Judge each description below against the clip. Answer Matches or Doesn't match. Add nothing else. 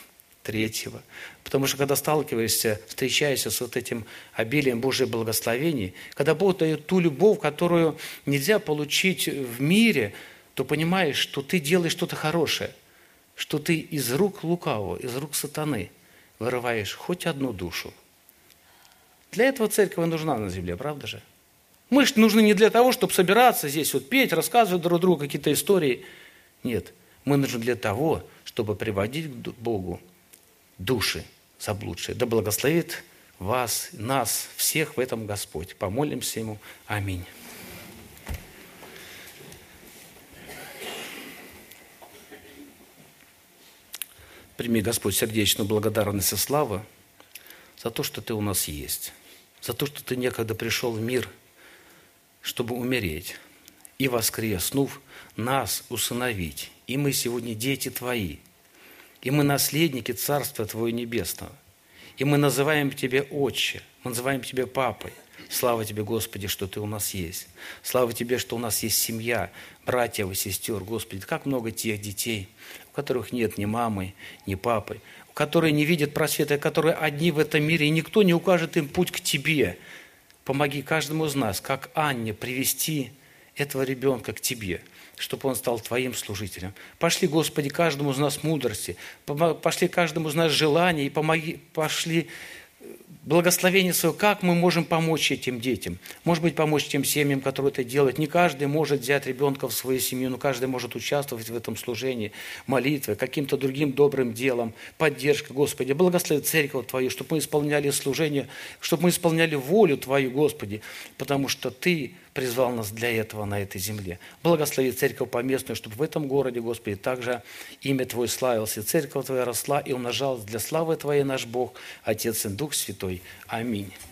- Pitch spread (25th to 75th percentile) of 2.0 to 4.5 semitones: Doesn't match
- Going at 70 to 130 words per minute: Doesn't match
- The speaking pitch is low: Matches